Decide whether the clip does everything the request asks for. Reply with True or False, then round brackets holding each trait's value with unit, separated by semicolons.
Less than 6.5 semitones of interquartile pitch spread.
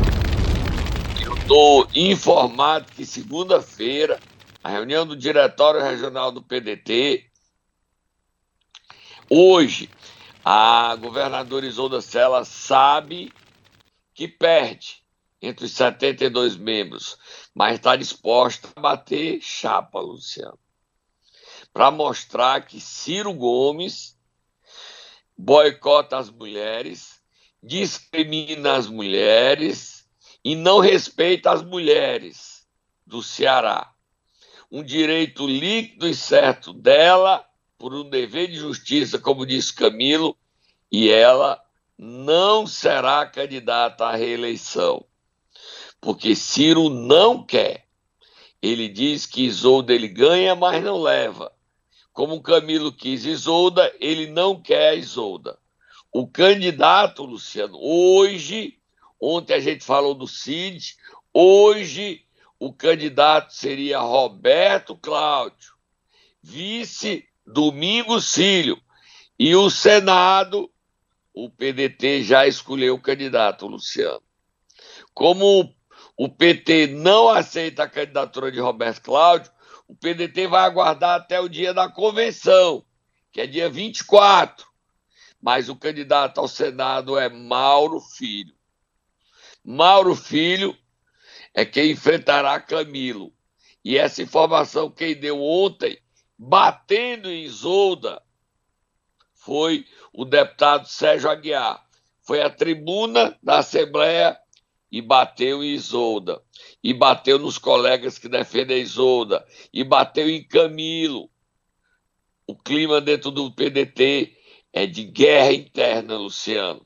False (7.7 semitones)